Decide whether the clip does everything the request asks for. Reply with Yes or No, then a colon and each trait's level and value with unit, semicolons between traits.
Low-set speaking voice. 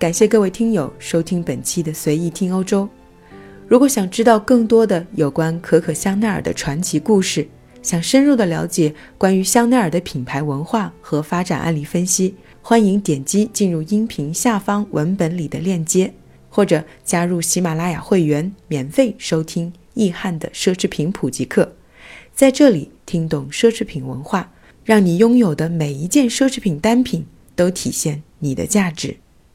No: medium, 175 Hz